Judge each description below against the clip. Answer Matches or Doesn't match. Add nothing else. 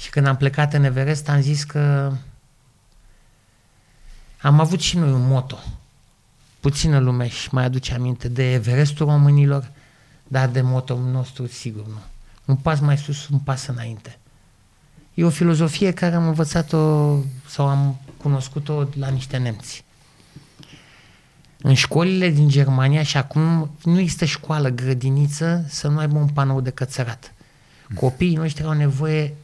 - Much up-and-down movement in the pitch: Doesn't match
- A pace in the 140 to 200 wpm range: Matches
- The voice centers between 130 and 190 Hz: Matches